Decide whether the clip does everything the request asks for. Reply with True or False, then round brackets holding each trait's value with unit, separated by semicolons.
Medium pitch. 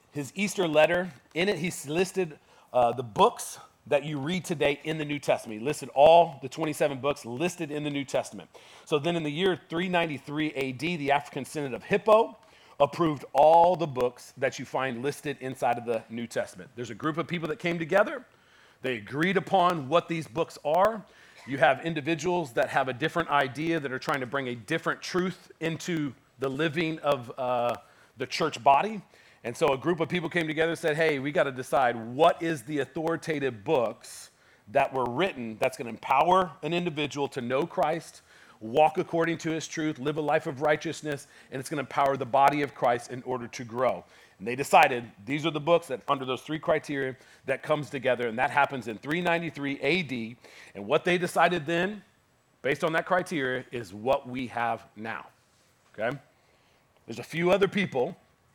True (150 Hz)